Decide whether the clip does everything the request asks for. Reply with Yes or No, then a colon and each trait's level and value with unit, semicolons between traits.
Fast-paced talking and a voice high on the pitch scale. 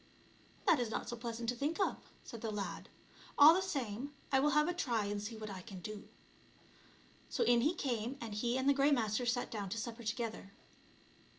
Yes: fast, 220 wpm; high, 235 Hz